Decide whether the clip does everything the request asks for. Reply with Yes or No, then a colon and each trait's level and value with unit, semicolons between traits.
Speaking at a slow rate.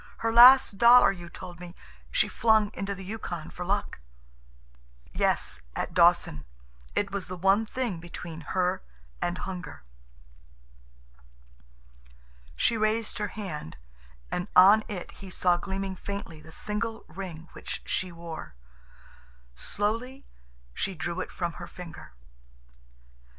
Yes: slow, 125 wpm